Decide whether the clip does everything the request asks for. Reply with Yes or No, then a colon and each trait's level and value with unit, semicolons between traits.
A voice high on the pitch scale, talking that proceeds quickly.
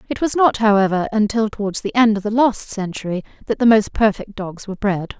Yes: high, 210 Hz; fast, 220 wpm